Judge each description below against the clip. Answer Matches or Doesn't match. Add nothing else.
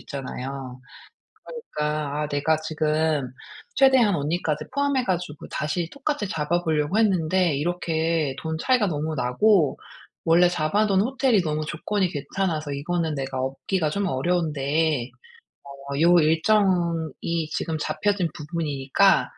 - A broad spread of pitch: Doesn't match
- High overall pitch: Doesn't match